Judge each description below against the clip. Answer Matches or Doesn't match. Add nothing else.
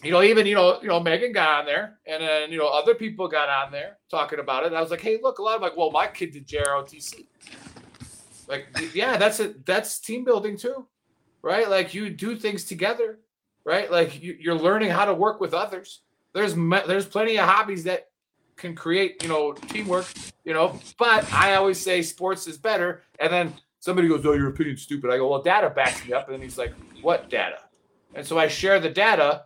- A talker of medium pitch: Matches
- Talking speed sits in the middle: Doesn't match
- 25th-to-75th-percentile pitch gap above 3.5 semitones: Matches